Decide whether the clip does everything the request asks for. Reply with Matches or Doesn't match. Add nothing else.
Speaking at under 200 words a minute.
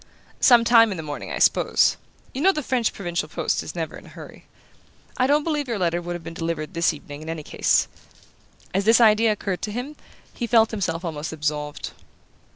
Doesn't match